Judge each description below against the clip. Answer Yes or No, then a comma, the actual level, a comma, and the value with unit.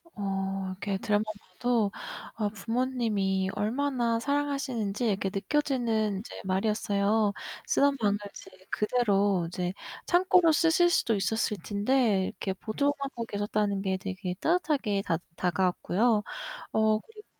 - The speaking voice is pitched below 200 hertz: No, high, 215 Hz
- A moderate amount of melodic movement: Yes, average, 4.4 semitones